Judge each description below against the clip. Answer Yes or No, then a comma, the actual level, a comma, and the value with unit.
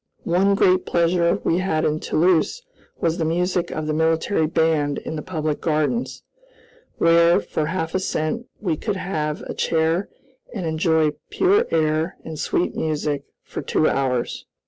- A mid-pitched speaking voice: Yes, medium, 165 Hz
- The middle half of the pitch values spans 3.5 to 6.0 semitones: No, narrow, 2.6 semitones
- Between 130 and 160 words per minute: Yes, average, 155 wpm